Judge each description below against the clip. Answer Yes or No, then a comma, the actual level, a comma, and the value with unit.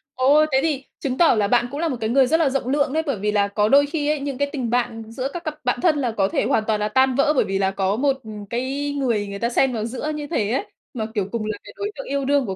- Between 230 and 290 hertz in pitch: Yes, very high, 255 Hz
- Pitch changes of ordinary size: Yes, average, 4.8 semitones